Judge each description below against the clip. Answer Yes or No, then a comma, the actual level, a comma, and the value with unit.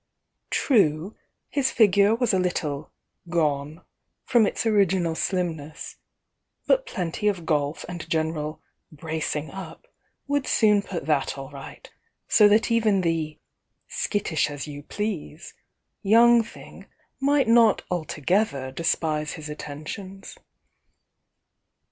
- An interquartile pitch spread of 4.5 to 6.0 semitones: Yes, wide, 5.5 semitones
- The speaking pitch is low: No, medium, 175 Hz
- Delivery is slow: Yes, slow, 115 wpm